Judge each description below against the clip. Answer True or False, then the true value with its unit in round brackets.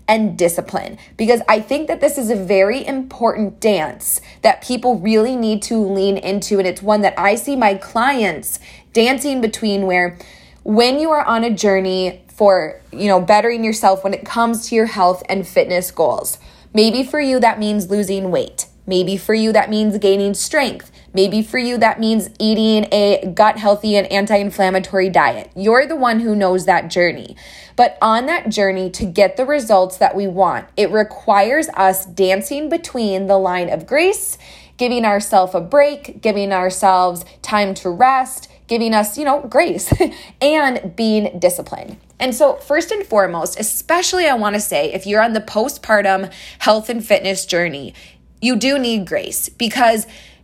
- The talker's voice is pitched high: True (210 Hz)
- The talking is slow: False (170 wpm)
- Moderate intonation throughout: True (3.9 semitones)